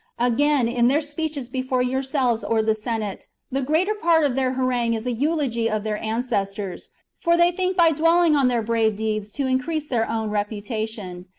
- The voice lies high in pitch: Yes, very high, 250 Hz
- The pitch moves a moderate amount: Yes, average, 5.0 semitones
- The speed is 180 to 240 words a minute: Yes, average, 185 wpm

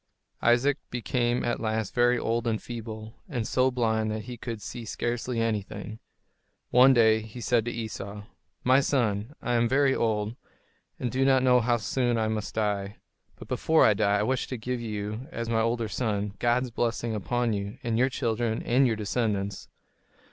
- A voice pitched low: Yes, low, 115 Hz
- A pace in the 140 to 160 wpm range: No, average, 185 wpm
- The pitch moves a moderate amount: No, narrow, 2.1 semitones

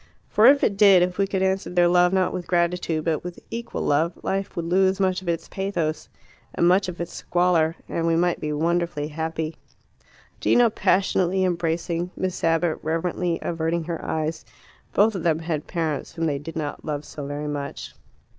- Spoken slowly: No, average, 185 wpm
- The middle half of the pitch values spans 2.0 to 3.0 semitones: Yes, narrow, 2.5 semitones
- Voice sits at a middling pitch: Yes, medium, 170 Hz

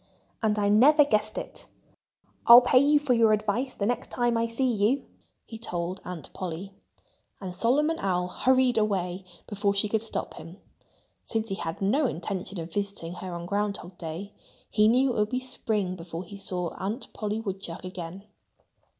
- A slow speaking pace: No, average, 175 wpm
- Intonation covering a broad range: No, average, 4.3 semitones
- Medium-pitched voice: No, high, 205 Hz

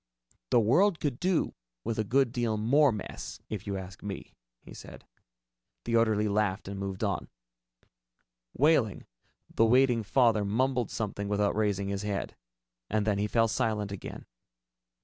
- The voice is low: Yes, low, 110 Hz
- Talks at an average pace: Yes, average, 150 wpm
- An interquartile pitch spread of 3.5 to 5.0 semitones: No, average, 3.1 semitones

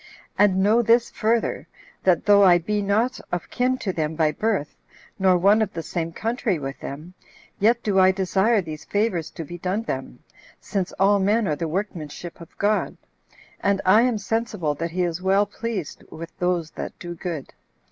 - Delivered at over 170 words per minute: Yes, average, 185 wpm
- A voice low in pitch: No, high, 190 Hz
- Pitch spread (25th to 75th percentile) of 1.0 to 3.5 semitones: No, average, 4.0 semitones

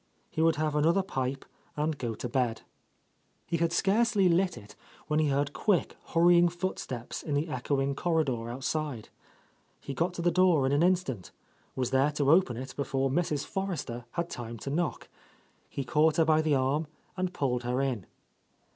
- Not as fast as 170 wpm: No, average, 180 wpm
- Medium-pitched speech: Yes, medium, 150 Hz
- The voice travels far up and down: No, average, 4.5 semitones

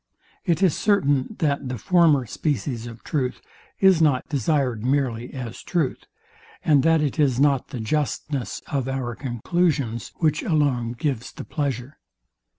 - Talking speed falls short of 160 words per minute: Yes, average, 145 wpm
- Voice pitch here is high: No, medium, 140 Hz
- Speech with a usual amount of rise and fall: Yes, average, 3.7 semitones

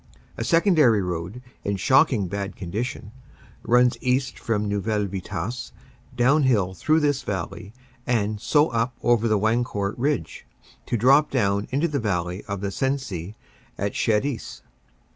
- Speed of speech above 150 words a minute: No, slow, 135 wpm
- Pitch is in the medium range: No, low, 115 Hz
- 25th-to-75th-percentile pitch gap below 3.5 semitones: No, average, 4.7 semitones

